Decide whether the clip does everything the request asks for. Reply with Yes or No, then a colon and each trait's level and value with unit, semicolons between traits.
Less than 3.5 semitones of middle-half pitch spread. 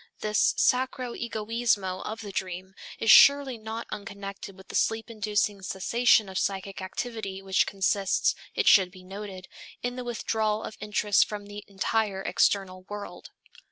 Yes: narrow, 2.6 semitones